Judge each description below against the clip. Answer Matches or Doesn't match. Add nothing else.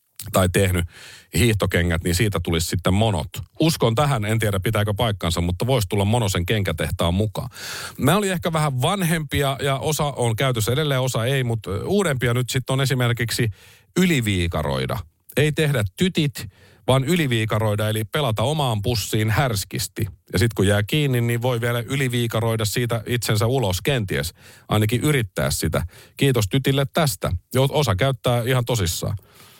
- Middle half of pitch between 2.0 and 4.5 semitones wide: Doesn't match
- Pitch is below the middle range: Matches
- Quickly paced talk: Doesn't match